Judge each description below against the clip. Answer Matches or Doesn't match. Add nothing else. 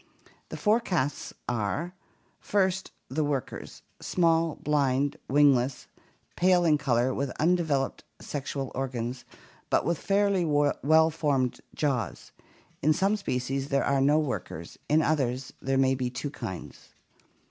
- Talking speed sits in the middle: Doesn't match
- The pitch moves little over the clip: Doesn't match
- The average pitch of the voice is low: Doesn't match